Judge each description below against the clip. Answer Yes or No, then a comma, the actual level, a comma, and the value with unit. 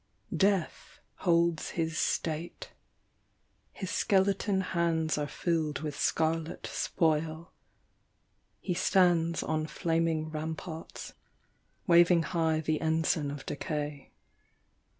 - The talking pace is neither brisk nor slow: No, slow, 90 wpm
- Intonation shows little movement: Yes, narrow, 1.5 semitones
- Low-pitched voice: No, medium, 165 Hz